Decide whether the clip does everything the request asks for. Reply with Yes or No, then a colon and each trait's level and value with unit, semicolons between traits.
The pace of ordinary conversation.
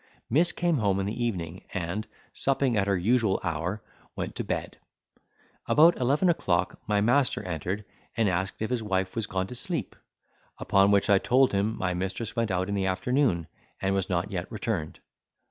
Yes: average, 180 wpm